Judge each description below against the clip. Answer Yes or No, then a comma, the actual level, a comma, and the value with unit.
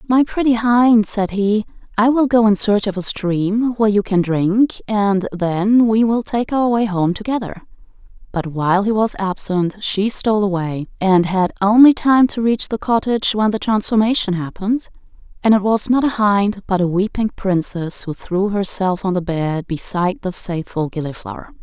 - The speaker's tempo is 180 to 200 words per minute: Yes, average, 185 wpm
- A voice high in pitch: Yes, high, 205 Hz